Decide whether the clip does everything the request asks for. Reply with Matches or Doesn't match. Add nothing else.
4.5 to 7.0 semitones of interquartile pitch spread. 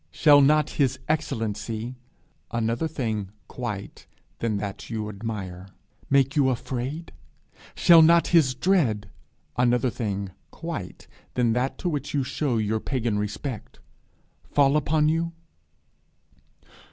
Matches